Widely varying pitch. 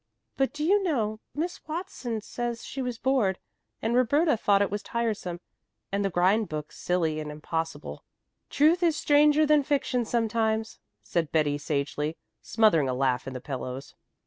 Yes: wide, 9.0 semitones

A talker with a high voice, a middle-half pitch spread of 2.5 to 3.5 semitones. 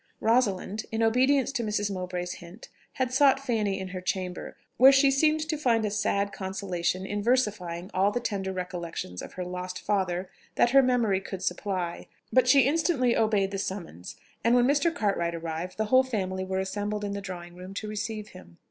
No: high, 205 Hz; average, 4.7 semitones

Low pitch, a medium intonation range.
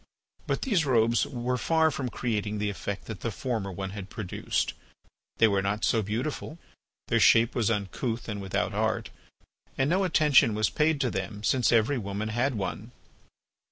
Yes: low, 115 Hz; average, 4.1 semitones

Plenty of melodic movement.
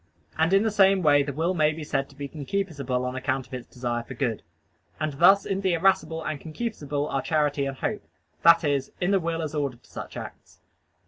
No: average, 3.7 semitones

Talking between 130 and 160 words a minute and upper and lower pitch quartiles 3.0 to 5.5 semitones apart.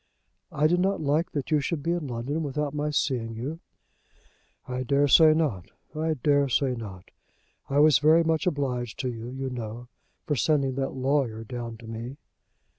No: average, 170 wpm; average, 3.9 semitones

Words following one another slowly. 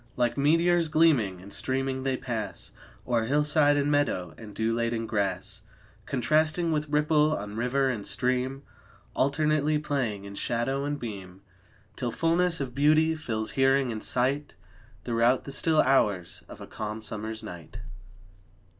No: average, 145 wpm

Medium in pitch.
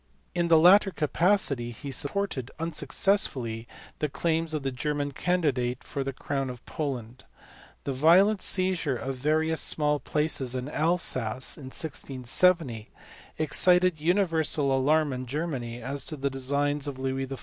Yes: medium, 145 Hz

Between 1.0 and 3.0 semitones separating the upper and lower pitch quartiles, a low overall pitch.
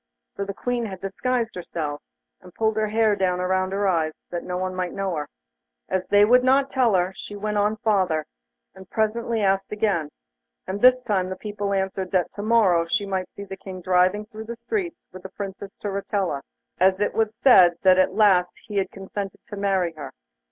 No: narrow, 2.5 semitones; high, 195 Hz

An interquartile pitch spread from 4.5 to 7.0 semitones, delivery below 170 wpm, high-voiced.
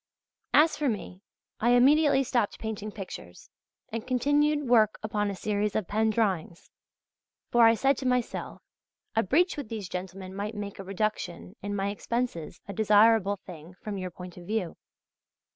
No: average, 3.8 semitones; average, 160 wpm; high, 215 Hz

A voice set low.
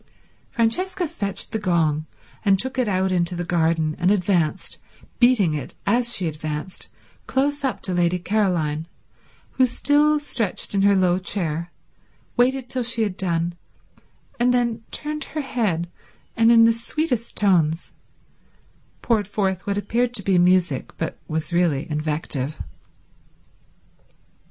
No: high, 195 Hz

